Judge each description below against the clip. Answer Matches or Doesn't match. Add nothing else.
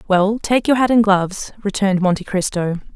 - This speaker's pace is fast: Doesn't match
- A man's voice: Doesn't match